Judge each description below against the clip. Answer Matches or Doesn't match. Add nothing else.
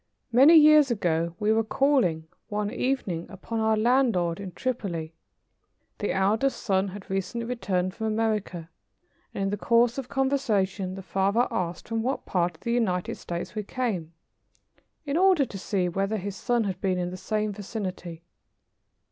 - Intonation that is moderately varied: Matches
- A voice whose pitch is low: Doesn't match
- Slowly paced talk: Doesn't match